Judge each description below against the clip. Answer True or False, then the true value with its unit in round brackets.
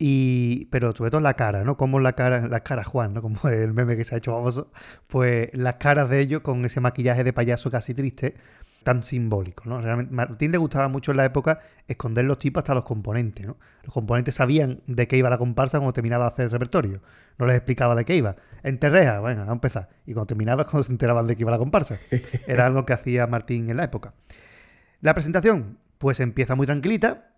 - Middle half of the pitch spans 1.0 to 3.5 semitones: True (2.5 semitones)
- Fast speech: True (225 wpm)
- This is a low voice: True (125 Hz)